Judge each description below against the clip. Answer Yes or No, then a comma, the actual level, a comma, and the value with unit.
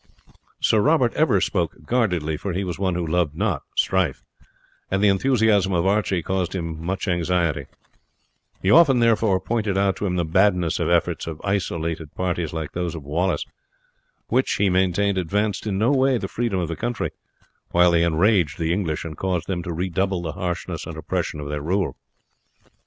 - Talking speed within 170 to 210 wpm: Yes, average, 180 wpm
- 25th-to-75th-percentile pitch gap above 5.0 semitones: No, average, 3.3 semitones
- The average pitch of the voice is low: Yes, very low, 90 Hz